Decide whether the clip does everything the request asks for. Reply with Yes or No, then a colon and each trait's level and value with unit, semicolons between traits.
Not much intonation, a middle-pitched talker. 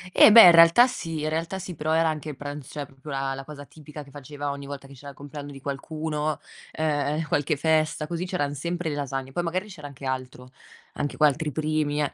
Yes: narrow, 2.1 semitones; medium, 150 Hz